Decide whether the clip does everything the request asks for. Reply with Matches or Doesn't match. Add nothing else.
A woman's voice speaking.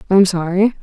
Matches